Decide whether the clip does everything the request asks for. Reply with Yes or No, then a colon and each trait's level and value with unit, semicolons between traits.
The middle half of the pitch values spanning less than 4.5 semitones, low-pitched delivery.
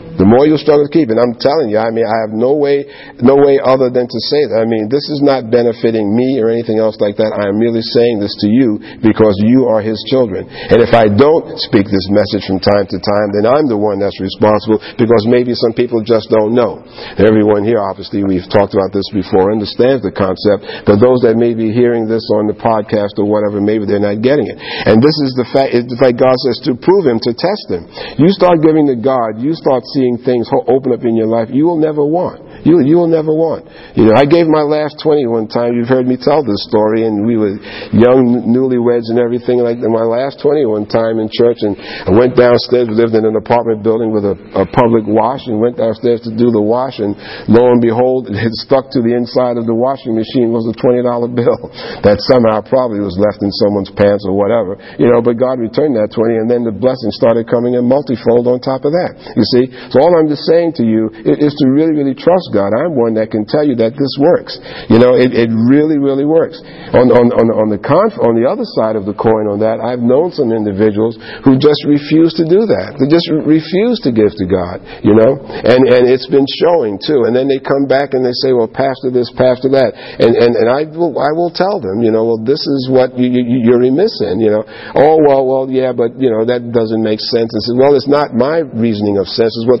Yes: average, 3.2 semitones; low, 120 Hz